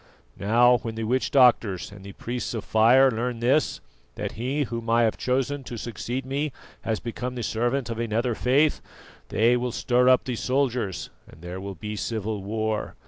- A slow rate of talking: No, average, 185 wpm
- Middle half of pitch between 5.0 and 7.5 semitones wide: No, narrow, 2.5 semitones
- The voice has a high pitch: No, low, 120 Hz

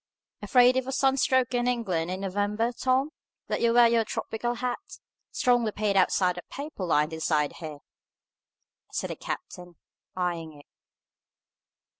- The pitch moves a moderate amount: No, wide, 5.7 semitones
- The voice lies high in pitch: Yes, high, 220 Hz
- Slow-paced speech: No, average, 145 wpm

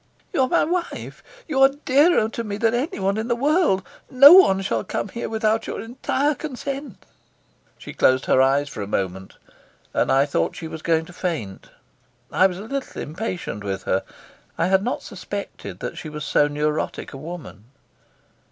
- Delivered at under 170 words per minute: No, average, 180 wpm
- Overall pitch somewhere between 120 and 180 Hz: No, high, 195 Hz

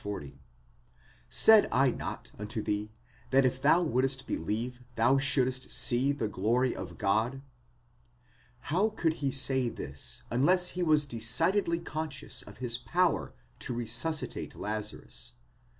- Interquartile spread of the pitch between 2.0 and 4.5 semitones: No, average, 5.1 semitones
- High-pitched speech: No, low, 130 Hz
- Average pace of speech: No, slow, 130 wpm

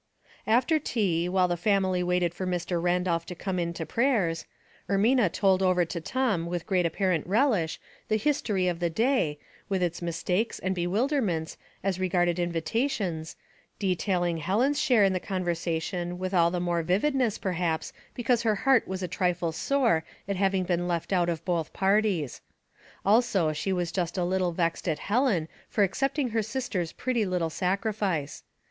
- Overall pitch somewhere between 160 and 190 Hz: Yes, medium, 185 Hz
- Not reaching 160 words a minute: No, average, 170 wpm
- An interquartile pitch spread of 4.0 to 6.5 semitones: No, average, 3.6 semitones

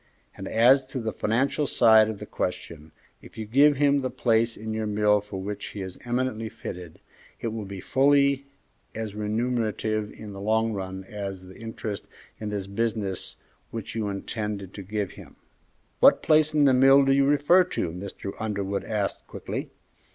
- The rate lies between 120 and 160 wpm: No, average, 175 wpm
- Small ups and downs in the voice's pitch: No, average, 4.1 semitones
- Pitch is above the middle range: No, low, 110 Hz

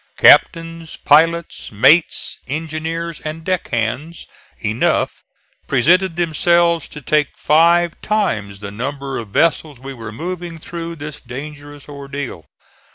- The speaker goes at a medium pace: No, slow, 115 wpm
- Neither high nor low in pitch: Yes, medium, 155 Hz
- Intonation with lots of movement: No, average, 3.7 semitones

